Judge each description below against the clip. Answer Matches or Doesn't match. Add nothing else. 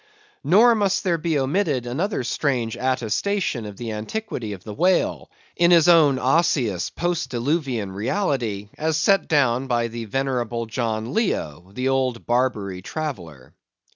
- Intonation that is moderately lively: Doesn't match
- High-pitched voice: Doesn't match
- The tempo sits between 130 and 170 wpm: Matches